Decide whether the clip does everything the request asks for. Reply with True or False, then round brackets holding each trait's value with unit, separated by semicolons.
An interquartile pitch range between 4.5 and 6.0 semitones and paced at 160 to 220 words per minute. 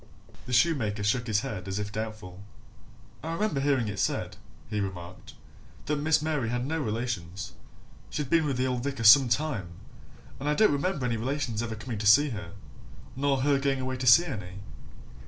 True (5.2 semitones; 185 wpm)